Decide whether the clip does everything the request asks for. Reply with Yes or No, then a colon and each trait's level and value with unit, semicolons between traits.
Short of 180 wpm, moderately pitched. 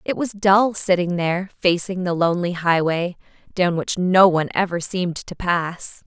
Yes: average, 165 wpm; medium, 180 Hz